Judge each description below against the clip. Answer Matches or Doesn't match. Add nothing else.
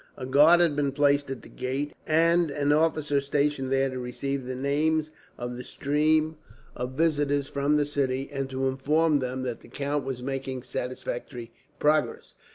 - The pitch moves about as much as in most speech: Doesn't match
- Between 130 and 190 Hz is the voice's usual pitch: Matches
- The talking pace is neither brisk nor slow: Matches